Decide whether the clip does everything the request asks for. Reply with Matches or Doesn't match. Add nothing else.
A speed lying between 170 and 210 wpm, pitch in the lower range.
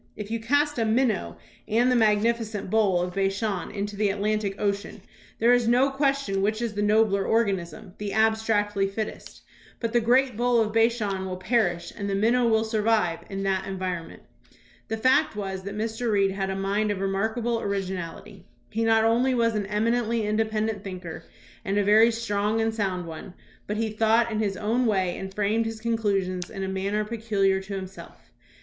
Doesn't match